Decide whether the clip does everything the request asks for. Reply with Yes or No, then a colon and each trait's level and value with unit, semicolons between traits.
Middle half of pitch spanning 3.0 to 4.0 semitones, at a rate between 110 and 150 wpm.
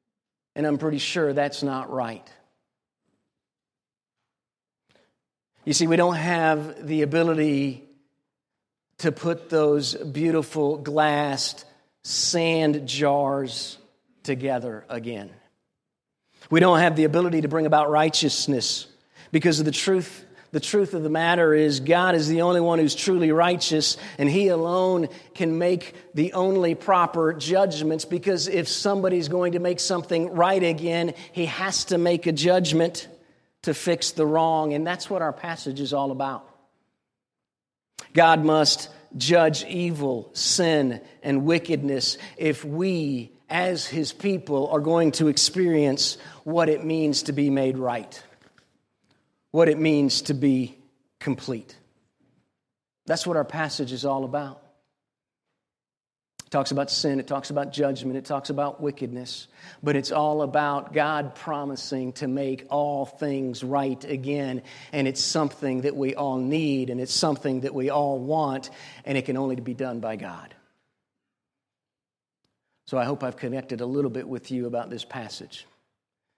Yes: average, 3.3 semitones; average, 140 wpm